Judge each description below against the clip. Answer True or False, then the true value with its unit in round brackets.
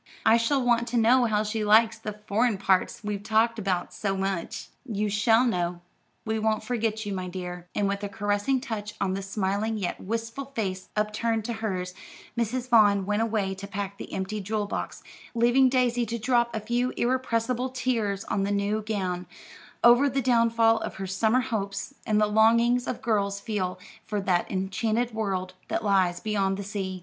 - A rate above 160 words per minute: True (185 wpm)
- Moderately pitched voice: False (215 Hz)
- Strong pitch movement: False (2.8 semitones)